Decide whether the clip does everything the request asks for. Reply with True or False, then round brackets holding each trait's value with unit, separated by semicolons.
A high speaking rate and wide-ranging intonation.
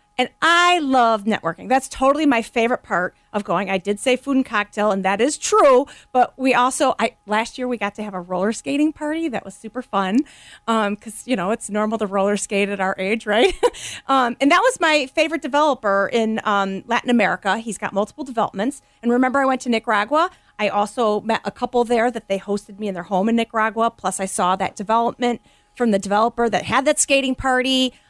False (215 wpm; 4.3 semitones)